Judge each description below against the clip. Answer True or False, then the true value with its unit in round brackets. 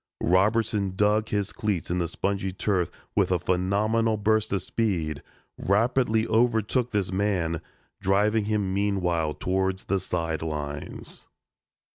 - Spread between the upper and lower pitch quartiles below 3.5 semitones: True (3.1 semitones)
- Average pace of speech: False (120 wpm)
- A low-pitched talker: True (100 Hz)